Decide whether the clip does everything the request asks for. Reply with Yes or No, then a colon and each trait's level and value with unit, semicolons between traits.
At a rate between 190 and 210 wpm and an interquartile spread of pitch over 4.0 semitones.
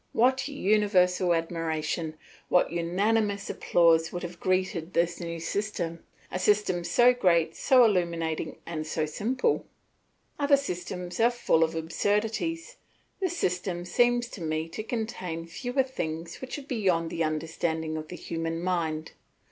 No: average, 140 wpm; average, 5.1 semitones